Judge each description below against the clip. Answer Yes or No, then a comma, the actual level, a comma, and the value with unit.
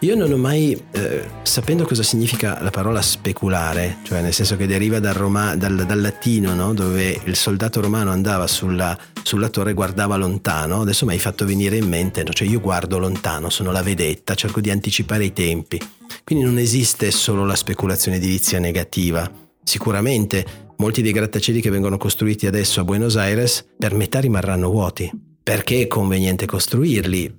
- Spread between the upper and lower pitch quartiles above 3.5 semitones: No, average, 2.7 semitones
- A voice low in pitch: Yes, low, 100 Hz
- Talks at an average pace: No, fast, 175 wpm